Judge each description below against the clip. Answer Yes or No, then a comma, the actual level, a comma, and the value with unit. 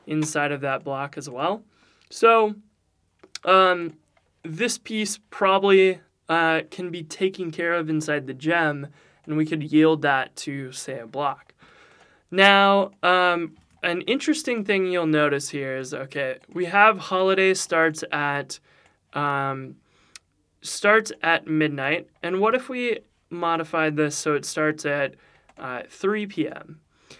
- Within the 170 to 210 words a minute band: No, slow, 135 wpm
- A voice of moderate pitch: Yes, medium, 165 Hz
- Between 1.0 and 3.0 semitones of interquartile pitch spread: No, average, 4.3 semitones